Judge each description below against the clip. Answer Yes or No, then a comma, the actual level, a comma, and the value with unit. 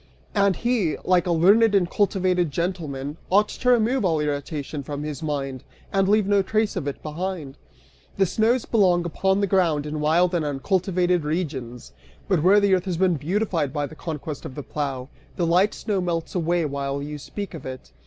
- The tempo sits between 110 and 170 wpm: No, average, 190 wpm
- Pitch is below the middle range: No, medium, 175 Hz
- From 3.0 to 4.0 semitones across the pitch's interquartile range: No, average, 4.5 semitones